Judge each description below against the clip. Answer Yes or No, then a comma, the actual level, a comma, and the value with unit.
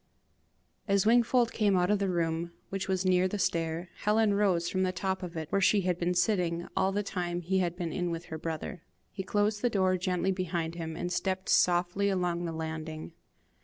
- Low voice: No, medium, 180 Hz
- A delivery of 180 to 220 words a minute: Yes, average, 200 wpm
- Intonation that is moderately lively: No, narrow, 2.3 semitones